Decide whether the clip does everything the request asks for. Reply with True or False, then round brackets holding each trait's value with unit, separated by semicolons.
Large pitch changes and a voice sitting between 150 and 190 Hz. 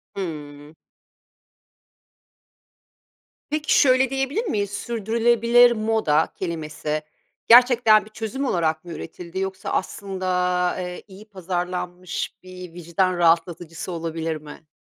False (4.9 semitones; 185 Hz)